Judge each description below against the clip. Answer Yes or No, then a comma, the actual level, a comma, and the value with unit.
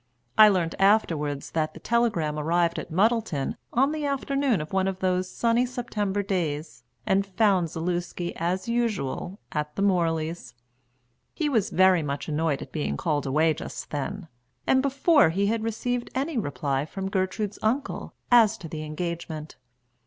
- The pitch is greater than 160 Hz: Yes, medium, 185 Hz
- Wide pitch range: Yes, wide, 5.9 semitones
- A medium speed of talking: Yes, average, 155 wpm